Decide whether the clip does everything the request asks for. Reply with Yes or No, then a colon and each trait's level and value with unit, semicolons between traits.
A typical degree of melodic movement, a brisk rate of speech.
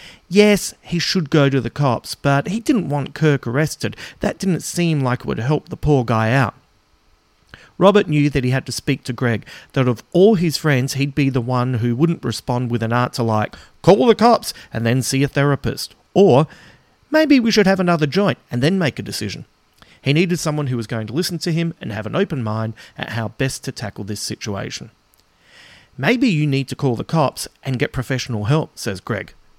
No: wide, 5.7 semitones; fast, 210 wpm